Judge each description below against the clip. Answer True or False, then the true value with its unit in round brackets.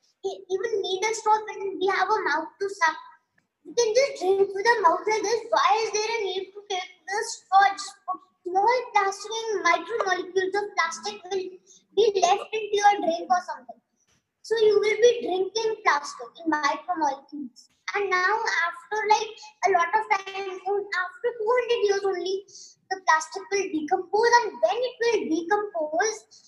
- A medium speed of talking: True (165 wpm)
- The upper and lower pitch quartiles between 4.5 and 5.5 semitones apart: False (3.0 semitones)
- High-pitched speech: True (390 Hz)